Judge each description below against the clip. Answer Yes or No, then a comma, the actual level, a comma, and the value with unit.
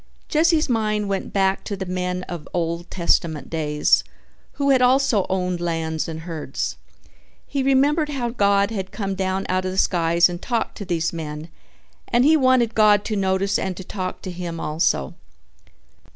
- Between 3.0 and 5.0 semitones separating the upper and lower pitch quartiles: Yes, average, 4.7 semitones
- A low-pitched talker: No, high, 190 Hz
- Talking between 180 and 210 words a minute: No, average, 170 wpm